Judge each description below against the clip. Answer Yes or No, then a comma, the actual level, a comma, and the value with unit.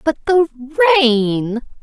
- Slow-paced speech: Yes, slow, 100 wpm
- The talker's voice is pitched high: Yes, very high, 275 Hz